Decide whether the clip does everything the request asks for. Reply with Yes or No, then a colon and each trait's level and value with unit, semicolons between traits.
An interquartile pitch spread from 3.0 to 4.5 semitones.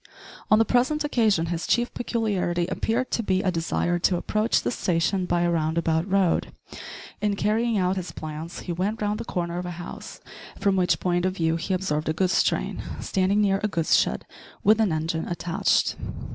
Yes: average, 3.6 semitones